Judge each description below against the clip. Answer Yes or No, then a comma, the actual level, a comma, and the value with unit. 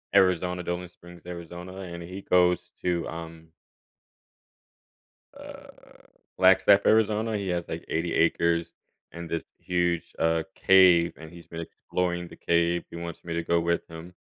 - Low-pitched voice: Yes, very low, 85 Hz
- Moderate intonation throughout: No, narrow, 1.2 semitones